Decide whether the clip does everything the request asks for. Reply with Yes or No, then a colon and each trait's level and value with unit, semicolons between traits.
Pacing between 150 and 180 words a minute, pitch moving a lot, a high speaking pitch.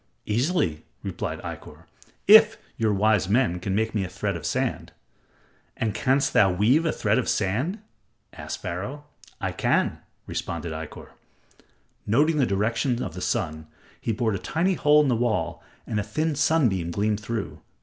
No: average, 160 wpm; wide, 5.7 semitones; low, 110 Hz